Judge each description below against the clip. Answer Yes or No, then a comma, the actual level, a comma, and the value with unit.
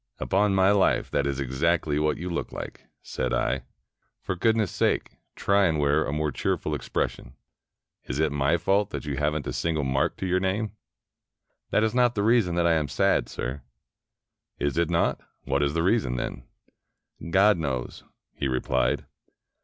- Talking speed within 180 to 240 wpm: Yes, average, 185 wpm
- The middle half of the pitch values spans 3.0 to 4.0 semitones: No, wide, 5.4 semitones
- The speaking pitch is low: Yes, very low, 80 Hz